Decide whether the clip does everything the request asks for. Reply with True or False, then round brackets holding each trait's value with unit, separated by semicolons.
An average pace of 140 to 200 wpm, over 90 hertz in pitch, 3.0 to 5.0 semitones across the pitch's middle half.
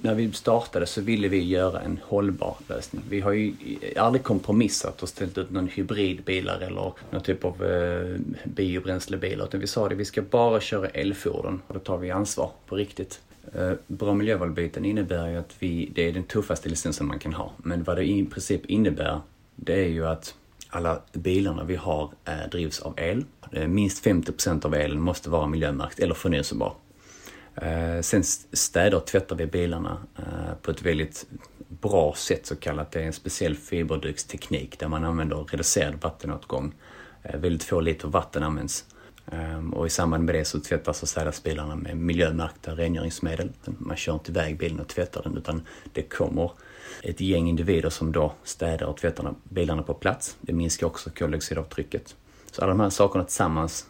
False (175 wpm; 85 Hz; 3.3 semitones)